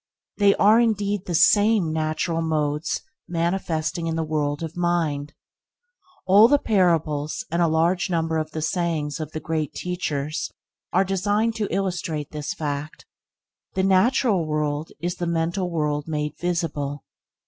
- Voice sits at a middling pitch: Yes, medium, 165 Hz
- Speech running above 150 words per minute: No, average, 145 wpm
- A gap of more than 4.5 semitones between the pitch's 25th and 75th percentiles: No, average, 3.3 semitones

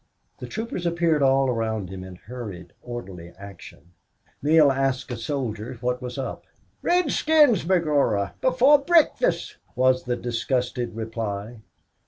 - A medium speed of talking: No, slow, 125 wpm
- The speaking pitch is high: No, low, 125 Hz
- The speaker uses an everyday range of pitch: No, wide, 6.4 semitones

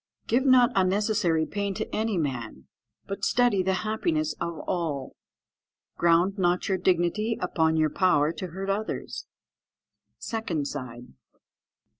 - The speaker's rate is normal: No, slow, 125 wpm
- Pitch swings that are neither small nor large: Yes, average, 4.3 semitones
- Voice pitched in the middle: Yes, medium, 180 Hz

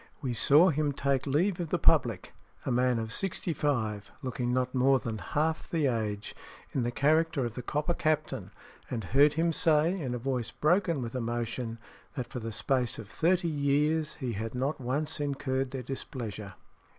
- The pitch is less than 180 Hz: Yes, low, 135 Hz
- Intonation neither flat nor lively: Yes, average, 4.2 semitones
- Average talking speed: Yes, average, 180 wpm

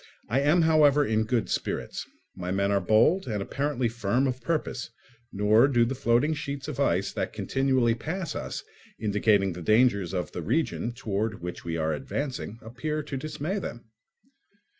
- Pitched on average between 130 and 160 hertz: No, low, 120 Hz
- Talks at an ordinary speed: Yes, average, 165 wpm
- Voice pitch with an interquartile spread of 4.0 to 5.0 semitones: No, wide, 5.5 semitones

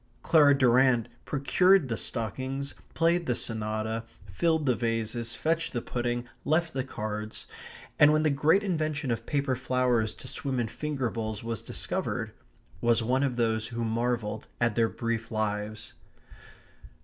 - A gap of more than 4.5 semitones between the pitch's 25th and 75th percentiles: No, average, 3.9 semitones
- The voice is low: Yes, low, 120 Hz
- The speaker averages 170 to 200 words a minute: No, average, 150 wpm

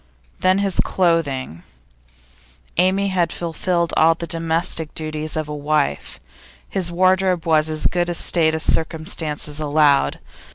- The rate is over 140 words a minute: No, slow, 135 wpm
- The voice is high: No, medium, 165 Hz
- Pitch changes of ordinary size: No, narrow, 2.3 semitones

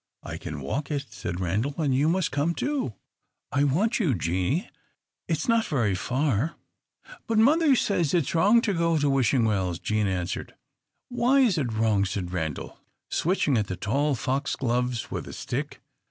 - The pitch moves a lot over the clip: Yes, wide, 8.3 semitones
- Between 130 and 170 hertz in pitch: Yes, medium, 140 Hz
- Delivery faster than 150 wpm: Yes, average, 180 wpm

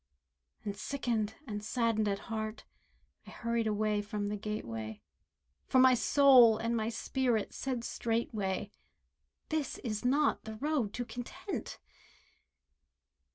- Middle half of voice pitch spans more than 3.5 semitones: No, average, 2.9 semitones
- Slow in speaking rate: Yes, slow, 120 wpm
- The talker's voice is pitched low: No, high, 225 Hz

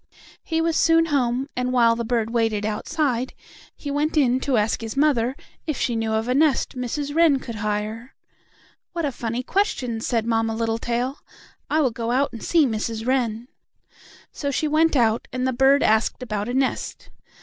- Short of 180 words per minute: No, average, 185 wpm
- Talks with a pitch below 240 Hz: No, very high, 250 Hz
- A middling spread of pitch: Yes, average, 3.9 semitones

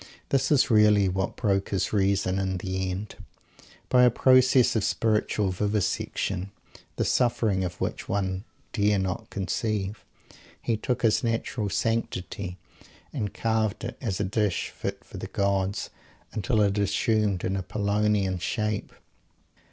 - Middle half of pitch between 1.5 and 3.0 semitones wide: Yes, narrow, 2.6 semitones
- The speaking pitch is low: Yes, low, 105 Hz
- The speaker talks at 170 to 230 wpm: No, slow, 135 wpm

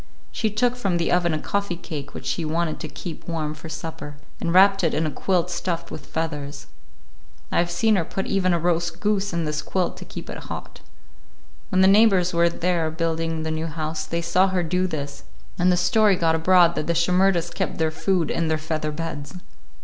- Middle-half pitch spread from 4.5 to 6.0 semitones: No, narrow, 2.5 semitones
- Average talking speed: No, fast, 210 wpm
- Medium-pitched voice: Yes, medium, 170 Hz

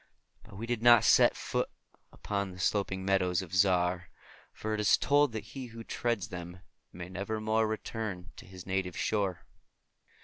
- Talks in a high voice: No, low, 100 Hz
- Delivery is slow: No, average, 165 wpm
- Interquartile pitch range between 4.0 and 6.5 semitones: No, average, 3.3 semitones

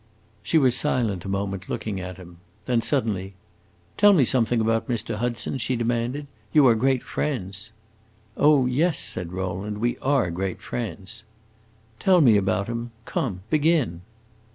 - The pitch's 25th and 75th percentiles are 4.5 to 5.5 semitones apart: Yes, average, 5.1 semitones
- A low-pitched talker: Yes, low, 115 Hz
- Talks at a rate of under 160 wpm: Yes, average, 150 wpm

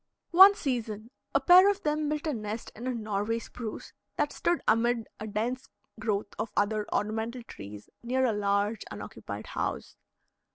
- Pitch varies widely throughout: No, average, 3.5 semitones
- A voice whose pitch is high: Yes, high, 230 Hz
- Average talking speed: Yes, average, 160 wpm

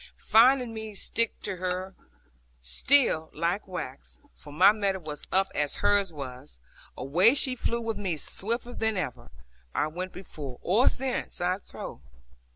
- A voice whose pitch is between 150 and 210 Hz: Yes, high, 190 Hz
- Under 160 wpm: Yes, average, 150 wpm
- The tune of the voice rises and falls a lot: Yes, wide, 6.3 semitones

